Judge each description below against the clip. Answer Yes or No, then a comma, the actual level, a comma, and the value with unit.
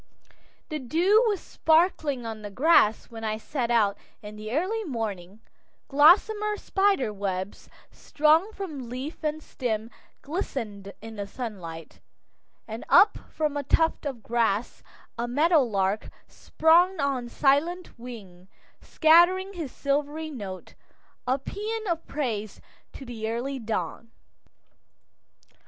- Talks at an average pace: No, slow, 125 wpm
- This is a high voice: Yes, very high, 265 Hz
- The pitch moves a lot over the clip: Yes, wide, 6.7 semitones